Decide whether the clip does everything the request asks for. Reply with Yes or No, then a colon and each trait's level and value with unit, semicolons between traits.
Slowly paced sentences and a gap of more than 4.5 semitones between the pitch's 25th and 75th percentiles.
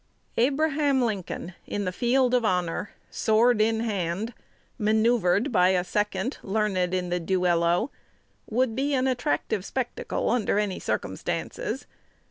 Yes: slow, 125 wpm; average, 5.2 semitones